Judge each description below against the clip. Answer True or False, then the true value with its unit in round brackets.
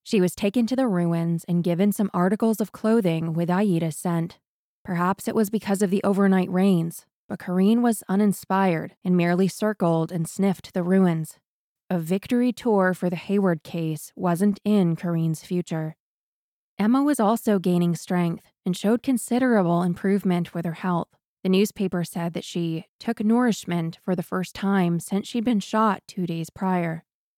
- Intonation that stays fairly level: False (3.2 semitones)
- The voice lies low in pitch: False (185 Hz)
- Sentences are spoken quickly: False (165 wpm)